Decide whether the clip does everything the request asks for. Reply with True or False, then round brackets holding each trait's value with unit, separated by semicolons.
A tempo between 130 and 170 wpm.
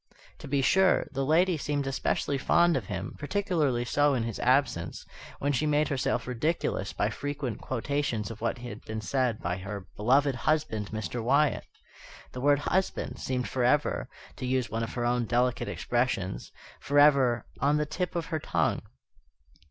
True (165 wpm)